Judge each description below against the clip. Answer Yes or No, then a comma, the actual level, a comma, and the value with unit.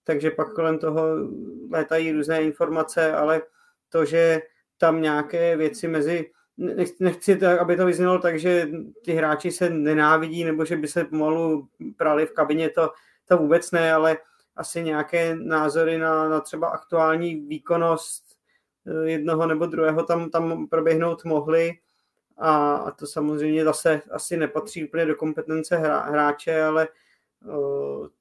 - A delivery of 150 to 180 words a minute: No, average, 140 wpm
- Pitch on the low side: No, medium, 160 Hz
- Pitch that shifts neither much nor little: No, narrow, 1.3 semitones